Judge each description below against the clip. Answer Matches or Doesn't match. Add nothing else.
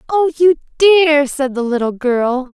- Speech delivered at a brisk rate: Doesn't match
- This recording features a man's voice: Doesn't match